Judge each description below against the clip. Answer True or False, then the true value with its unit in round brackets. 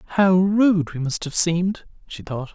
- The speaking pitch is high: False (175 Hz)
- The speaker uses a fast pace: False (190 wpm)